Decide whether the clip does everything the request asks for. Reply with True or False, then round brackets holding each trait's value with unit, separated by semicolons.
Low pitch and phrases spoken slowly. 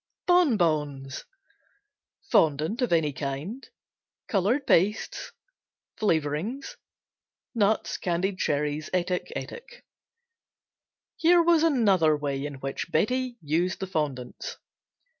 False (175 Hz; 95 wpm)